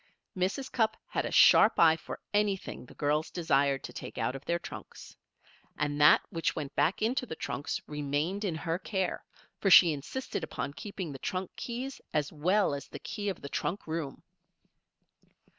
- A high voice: No, medium, 165 Hz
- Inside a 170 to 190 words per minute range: Yes, average, 175 wpm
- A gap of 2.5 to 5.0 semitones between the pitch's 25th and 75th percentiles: No, wide, 5.5 semitones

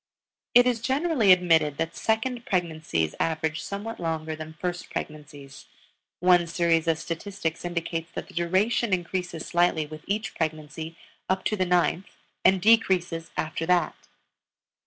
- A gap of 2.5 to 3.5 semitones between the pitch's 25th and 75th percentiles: Yes, average, 3.1 semitones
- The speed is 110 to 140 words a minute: Yes, slow, 135 wpm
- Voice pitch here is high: No, medium, 170 Hz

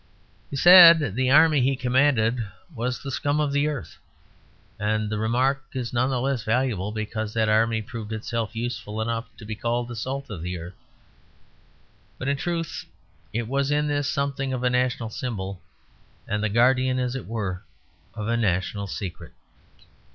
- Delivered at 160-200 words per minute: Yes, average, 170 wpm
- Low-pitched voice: Yes, low, 120 Hz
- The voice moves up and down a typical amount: Yes, average, 3.8 semitones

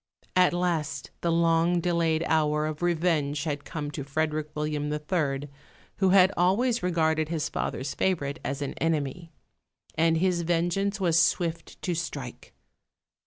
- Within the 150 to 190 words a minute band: No, average, 140 wpm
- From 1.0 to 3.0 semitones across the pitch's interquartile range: Yes, average, 2.7 semitones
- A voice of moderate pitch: Yes, medium, 165 Hz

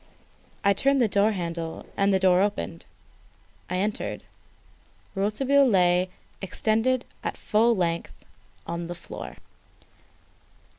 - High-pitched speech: Yes, high, 195 Hz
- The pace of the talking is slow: Yes, slow, 110 wpm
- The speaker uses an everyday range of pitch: Yes, average, 3.7 semitones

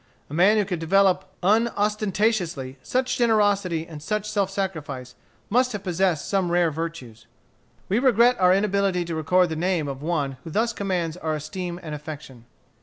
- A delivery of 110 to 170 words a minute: Yes, average, 165 wpm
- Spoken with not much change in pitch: No, average, 4.5 semitones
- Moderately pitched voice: Yes, medium, 180 Hz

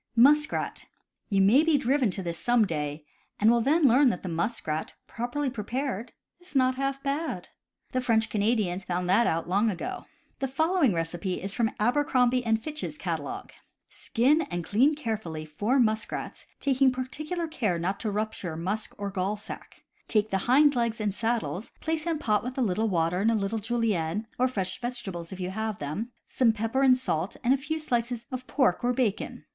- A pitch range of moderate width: Yes, average, 5.0 semitones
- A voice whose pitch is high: Yes, high, 230 Hz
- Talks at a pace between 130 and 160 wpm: No, average, 185 wpm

